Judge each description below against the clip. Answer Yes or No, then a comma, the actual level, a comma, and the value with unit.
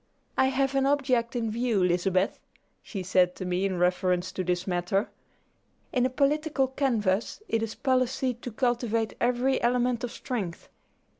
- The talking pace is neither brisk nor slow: Yes, average, 155 wpm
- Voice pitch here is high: Yes, high, 235 Hz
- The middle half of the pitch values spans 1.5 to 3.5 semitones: No, wide, 5.5 semitones